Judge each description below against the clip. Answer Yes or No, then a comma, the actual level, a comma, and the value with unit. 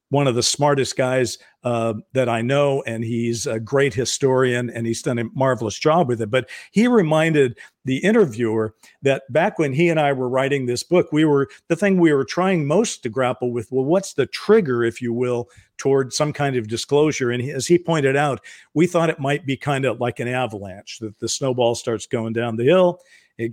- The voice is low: Yes, low, 130 Hz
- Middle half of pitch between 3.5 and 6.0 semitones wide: Yes, average, 4.1 semitones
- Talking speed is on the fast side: Yes, fast, 210 wpm